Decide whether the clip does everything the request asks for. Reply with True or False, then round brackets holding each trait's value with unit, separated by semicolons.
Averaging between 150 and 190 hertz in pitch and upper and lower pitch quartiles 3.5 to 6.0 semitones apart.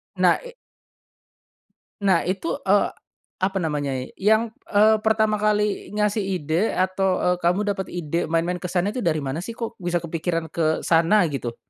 True (185 Hz; 4.1 semitones)